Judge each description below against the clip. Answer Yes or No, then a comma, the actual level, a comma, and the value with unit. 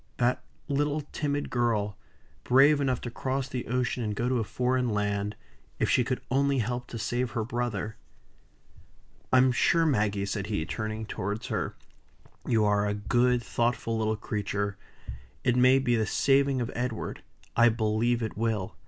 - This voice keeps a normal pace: Yes, average, 160 wpm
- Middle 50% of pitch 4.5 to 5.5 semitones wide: No, average, 3.0 semitones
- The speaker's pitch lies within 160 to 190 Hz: No, low, 120 Hz